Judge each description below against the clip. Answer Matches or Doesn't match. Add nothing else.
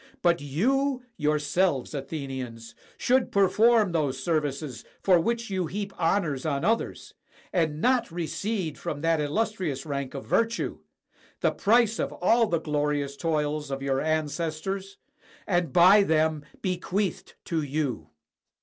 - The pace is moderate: Doesn't match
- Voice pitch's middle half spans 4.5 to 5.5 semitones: Matches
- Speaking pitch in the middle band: Matches